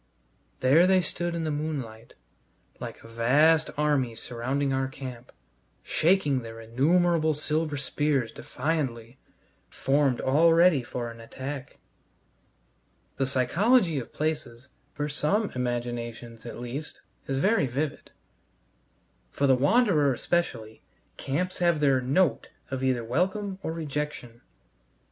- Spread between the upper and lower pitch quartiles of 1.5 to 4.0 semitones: No, average, 4.6 semitones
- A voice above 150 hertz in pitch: No, medium, 140 Hz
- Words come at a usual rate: No, slow, 120 wpm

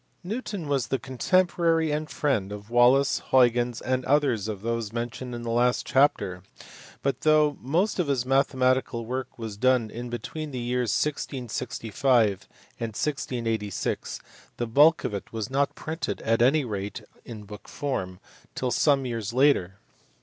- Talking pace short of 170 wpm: Yes, average, 150 wpm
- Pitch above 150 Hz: No, low, 125 Hz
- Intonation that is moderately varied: Yes, average, 3.9 semitones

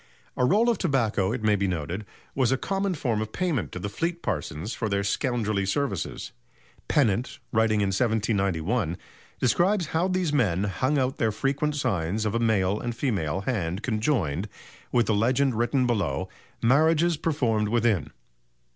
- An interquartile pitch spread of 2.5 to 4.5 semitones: No, wide, 5.6 semitones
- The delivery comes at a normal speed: Yes, average, 160 wpm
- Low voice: Yes, low, 115 Hz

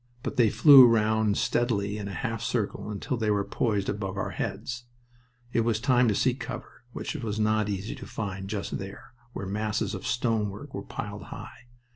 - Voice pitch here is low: Yes, low, 110 Hz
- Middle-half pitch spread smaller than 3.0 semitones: Yes, narrow, 2.6 semitones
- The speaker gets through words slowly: No, average, 185 wpm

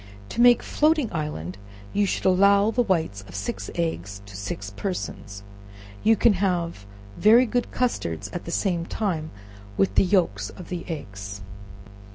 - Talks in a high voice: No, medium, 170 Hz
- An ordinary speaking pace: Yes, average, 155 wpm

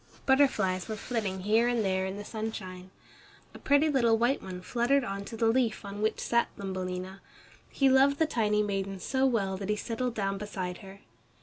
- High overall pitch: Yes, high, 210 Hz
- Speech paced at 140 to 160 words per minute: No, average, 190 wpm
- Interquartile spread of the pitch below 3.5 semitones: No, average, 3.9 semitones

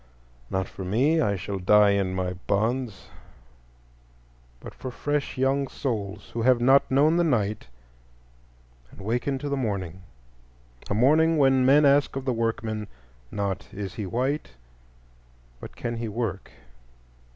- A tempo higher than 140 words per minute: No, slow, 135 wpm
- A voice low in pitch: Yes, low, 110 Hz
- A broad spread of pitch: Yes, wide, 5.8 semitones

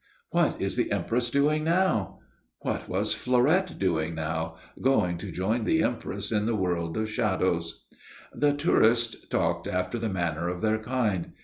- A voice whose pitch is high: No, low, 110 Hz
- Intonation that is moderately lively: No, wide, 6.0 semitones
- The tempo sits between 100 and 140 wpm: No, average, 155 wpm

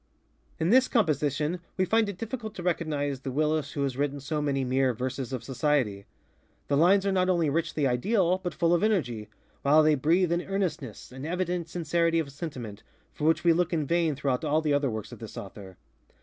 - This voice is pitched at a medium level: Yes, medium, 155 Hz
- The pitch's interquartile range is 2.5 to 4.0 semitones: No, average, 4.5 semitones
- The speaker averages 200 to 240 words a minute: Yes, fast, 205 wpm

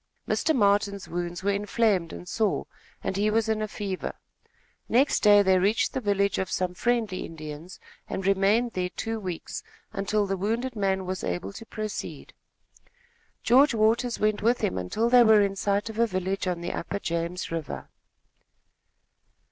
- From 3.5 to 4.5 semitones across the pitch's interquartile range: No, average, 3.1 semitones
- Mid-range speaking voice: No, high, 200 Hz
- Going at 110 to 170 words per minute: Yes, average, 165 wpm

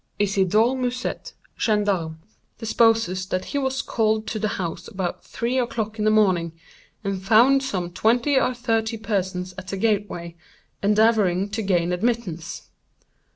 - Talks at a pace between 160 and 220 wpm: No, average, 140 wpm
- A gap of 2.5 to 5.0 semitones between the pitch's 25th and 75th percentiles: Yes, average, 3.6 semitones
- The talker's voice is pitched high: Yes, high, 210 Hz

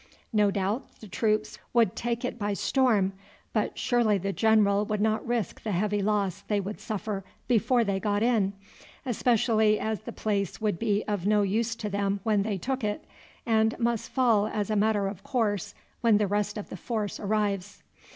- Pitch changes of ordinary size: No, narrow, 1.9 semitones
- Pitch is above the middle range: Yes, high, 210 Hz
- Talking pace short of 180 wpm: No, average, 185 wpm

